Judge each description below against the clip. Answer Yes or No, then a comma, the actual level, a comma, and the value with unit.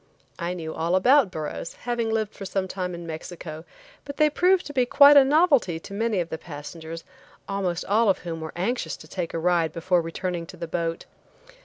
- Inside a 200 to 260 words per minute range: Yes, fast, 205 wpm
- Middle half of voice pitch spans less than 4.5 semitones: No, wide, 5.5 semitones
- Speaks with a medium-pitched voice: Yes, medium, 180 Hz